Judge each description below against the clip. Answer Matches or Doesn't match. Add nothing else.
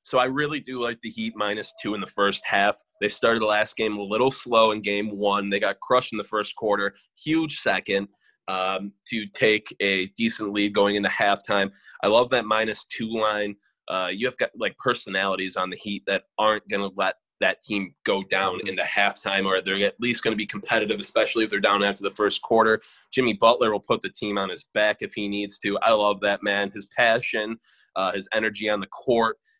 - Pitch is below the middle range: Matches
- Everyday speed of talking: Doesn't match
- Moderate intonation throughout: Doesn't match